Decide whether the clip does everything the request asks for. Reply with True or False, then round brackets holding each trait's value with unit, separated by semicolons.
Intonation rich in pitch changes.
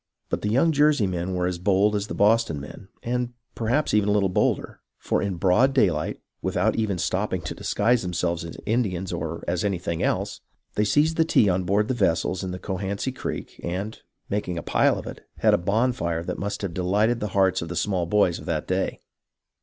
False (3.5 semitones)